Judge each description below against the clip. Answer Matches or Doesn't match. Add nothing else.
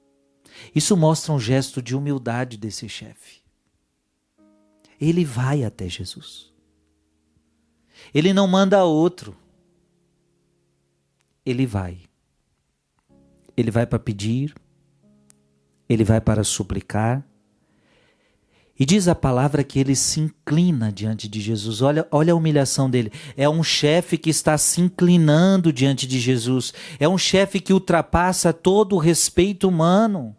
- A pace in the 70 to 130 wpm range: Matches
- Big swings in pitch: Matches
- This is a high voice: Doesn't match